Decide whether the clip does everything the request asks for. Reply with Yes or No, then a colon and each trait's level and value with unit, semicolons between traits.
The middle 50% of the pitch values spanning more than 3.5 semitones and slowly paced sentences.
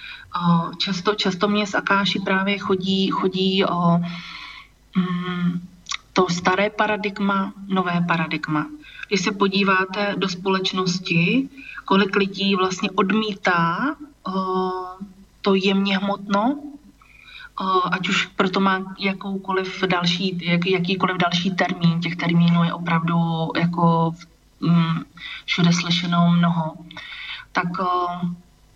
No: narrow, 2.4 semitones; slow, 100 wpm